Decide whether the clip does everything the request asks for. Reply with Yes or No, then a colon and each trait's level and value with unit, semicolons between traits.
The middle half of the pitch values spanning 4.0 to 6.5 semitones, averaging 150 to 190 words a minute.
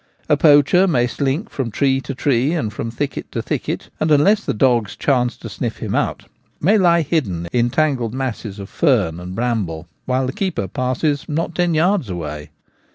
Yes: wide, 5.5 semitones; average, 185 wpm